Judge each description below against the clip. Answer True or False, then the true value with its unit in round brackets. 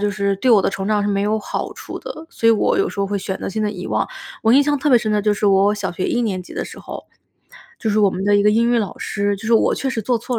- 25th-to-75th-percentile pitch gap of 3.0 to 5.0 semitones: False (2.5 semitones)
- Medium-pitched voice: False (210 Hz)